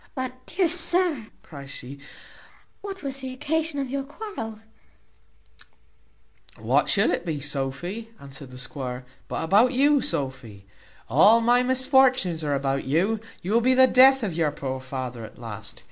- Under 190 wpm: Yes, average, 155 wpm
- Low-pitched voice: No, high, 215 Hz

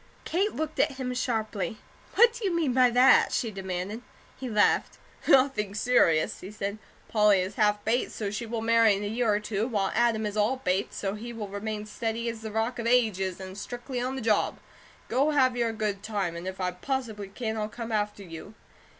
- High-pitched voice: Yes, high, 220 Hz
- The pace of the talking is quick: Yes, fast, 210 wpm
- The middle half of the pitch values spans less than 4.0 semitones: Yes, average, 3.2 semitones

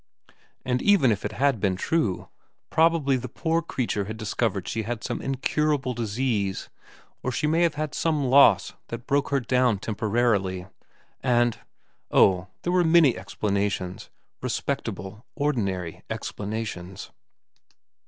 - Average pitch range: No, wide, 5.8 semitones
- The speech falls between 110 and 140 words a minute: Yes, slow, 135 wpm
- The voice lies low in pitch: Yes, low, 120 Hz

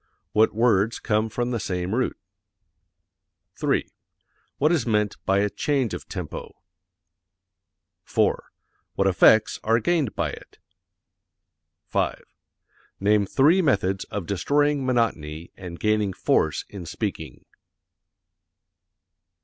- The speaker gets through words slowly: Yes, slow, 110 wpm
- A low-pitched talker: Yes, low, 105 Hz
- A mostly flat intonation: No, average, 4.3 semitones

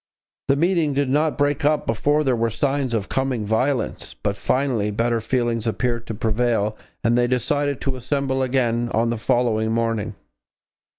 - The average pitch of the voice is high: No, low, 120 Hz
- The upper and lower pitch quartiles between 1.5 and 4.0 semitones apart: Yes, average, 3.3 semitones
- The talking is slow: No, average, 165 wpm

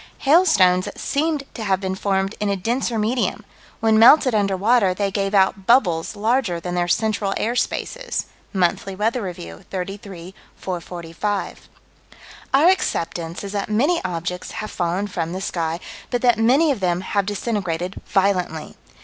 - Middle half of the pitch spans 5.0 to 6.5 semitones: No, average, 4.0 semitones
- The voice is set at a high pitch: Yes, high, 200 Hz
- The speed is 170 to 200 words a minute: No, average, 155 wpm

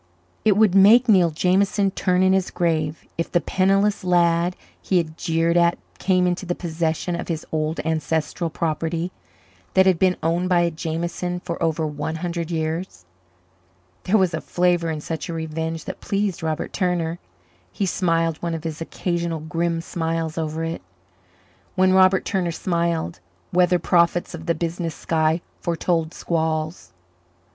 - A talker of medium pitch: Yes, medium, 170 Hz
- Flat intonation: Yes, narrow, 1.9 semitones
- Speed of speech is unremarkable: Yes, average, 155 wpm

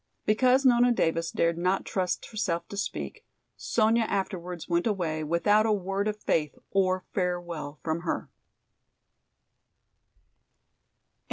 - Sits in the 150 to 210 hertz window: Yes, medium, 185 Hz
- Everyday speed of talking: No, slow, 115 wpm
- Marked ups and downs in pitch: No, average, 4.0 semitones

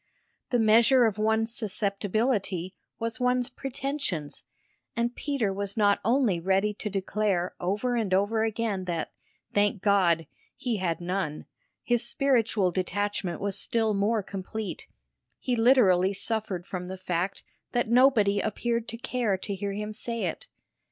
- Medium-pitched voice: No, high, 210 Hz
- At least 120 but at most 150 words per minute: Yes, average, 140 wpm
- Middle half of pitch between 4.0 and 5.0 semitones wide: No, average, 3.5 semitones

